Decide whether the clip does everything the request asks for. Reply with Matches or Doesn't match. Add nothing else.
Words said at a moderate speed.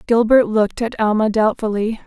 Matches